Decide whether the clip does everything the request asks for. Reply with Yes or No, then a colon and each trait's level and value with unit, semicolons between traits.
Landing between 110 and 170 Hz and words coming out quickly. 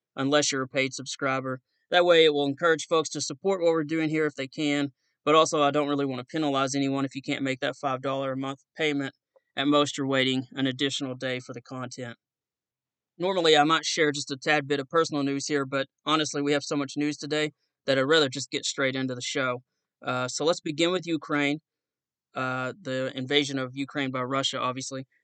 Yes: medium, 140 Hz; fast, 215 wpm